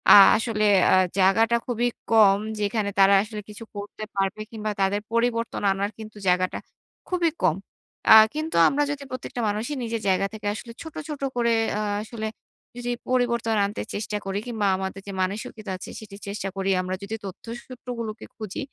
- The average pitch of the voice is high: Yes, high, 215 Hz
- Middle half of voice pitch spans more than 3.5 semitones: No, average, 3.0 semitones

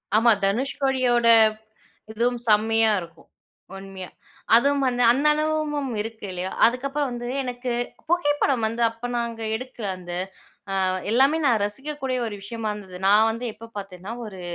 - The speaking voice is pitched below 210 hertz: No, high, 235 Hz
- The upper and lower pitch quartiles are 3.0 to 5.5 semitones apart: Yes, average, 4.0 semitones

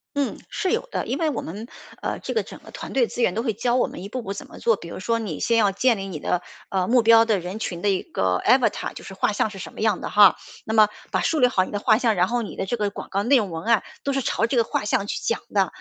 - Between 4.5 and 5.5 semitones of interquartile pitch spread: No, average, 3.7 semitones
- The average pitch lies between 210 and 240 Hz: Yes, high, 215 Hz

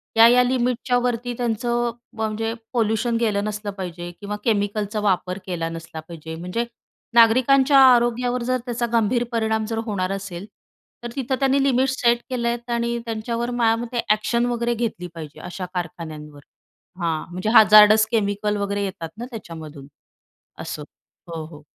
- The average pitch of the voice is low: No, high, 220 Hz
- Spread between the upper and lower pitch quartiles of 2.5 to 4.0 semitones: No, average, 4.4 semitones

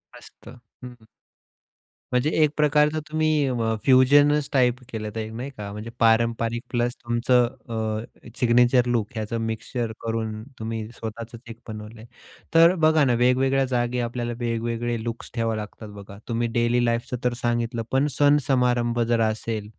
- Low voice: Yes, low, 120 Hz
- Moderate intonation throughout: No, narrow, 2.0 semitones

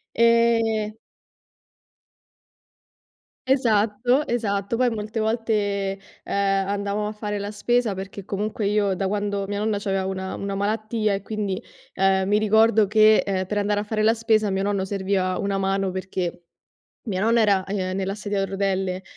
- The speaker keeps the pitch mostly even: Yes, narrow, 1.8 semitones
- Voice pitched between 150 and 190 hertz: No, high, 205 Hz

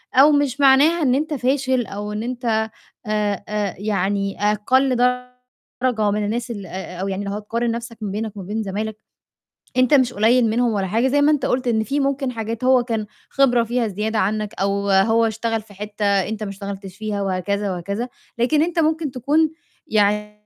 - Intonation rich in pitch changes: No, average, 3.7 semitones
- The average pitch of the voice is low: No, high, 220 Hz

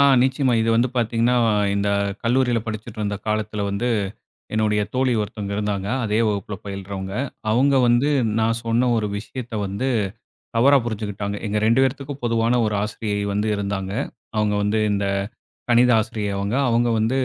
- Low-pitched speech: Yes, low, 110 Hz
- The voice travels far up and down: No, average, 2.8 semitones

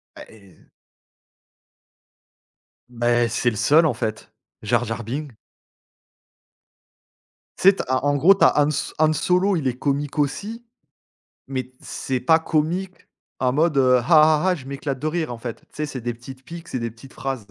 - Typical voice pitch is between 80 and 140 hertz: Yes, low, 135 Hz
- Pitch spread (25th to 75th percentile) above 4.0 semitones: Yes, average, 4.5 semitones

